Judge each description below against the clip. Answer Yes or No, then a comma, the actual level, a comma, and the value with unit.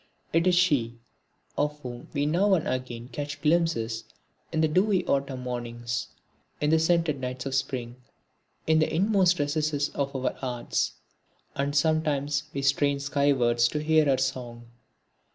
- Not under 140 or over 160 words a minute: Yes, average, 150 wpm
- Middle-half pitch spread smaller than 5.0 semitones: Yes, average, 3.8 semitones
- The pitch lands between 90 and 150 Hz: Yes, medium, 140 Hz